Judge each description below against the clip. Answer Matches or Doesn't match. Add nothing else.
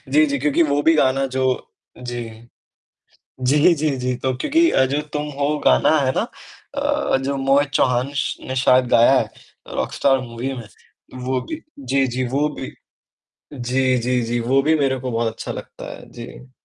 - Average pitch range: Doesn't match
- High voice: Doesn't match